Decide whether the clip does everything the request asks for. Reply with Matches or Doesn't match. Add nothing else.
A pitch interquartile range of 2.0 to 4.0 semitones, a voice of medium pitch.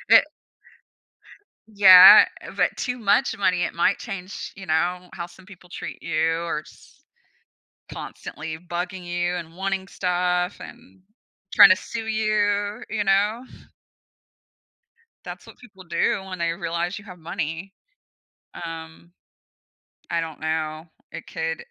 Matches